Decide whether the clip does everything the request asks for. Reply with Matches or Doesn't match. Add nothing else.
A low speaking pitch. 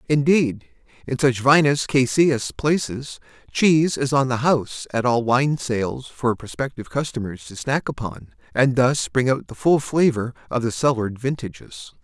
Matches